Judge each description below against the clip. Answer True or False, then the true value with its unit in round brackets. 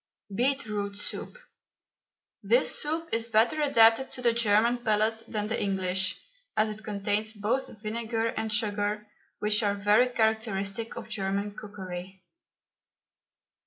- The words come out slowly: True (125 wpm)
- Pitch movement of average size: False (2.2 semitones)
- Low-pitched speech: False (215 Hz)